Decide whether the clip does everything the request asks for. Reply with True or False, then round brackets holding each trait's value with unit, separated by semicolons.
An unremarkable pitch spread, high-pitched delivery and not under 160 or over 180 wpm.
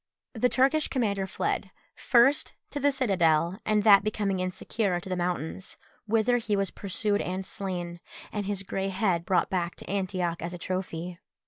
True (3.0 semitones; 195 Hz; 165 wpm)